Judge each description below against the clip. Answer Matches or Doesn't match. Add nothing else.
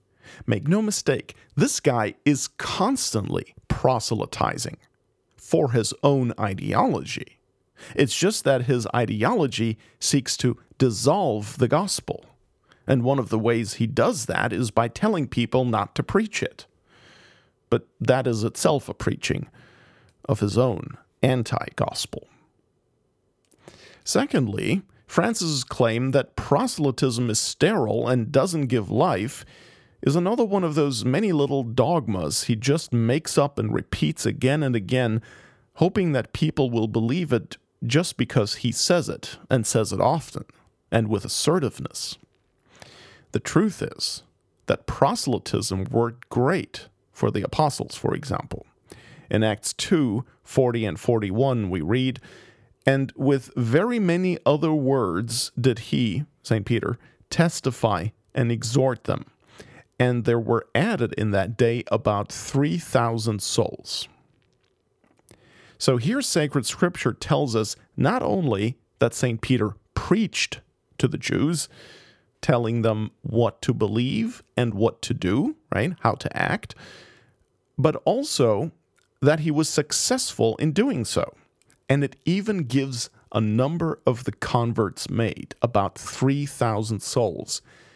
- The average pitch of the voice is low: Matches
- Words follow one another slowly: Matches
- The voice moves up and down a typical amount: Matches